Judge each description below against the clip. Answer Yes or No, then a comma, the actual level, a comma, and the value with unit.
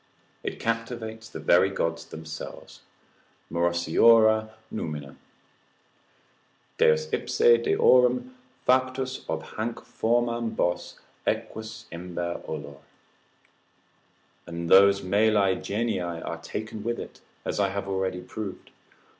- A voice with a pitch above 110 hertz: No, low, 100 Hz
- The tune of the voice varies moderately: Yes, average, 4.9 semitones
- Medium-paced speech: No, slow, 100 wpm